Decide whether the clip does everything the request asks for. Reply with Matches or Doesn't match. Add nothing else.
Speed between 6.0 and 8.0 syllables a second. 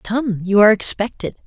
Doesn't match